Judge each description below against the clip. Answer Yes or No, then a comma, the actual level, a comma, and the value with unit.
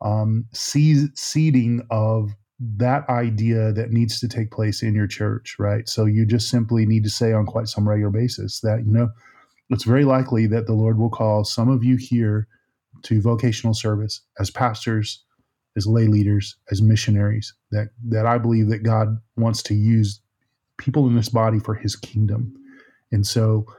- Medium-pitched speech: No, low, 110 Hz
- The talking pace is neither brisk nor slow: Yes, average, 175 wpm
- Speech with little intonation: Yes, narrow, 1.8 semitones